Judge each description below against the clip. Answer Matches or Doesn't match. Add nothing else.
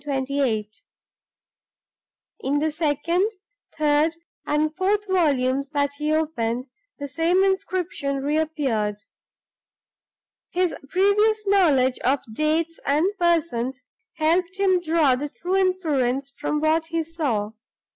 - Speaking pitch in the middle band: Doesn't match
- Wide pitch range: Doesn't match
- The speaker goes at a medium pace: Doesn't match